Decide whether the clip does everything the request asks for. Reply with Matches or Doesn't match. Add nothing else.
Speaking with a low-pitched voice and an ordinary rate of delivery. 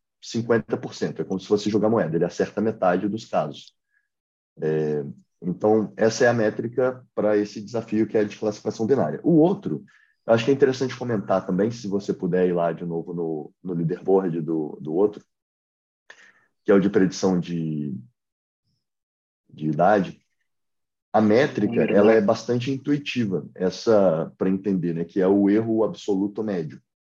Matches